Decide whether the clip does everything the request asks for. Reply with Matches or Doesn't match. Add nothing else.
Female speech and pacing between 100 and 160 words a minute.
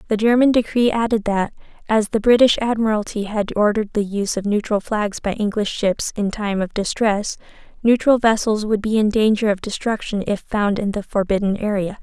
Doesn't match